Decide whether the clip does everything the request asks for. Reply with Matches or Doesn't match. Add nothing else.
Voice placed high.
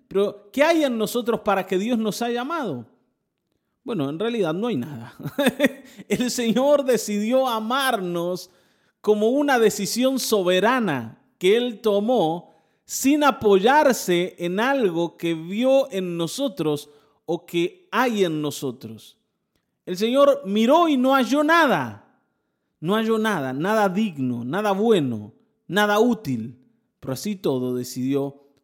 Matches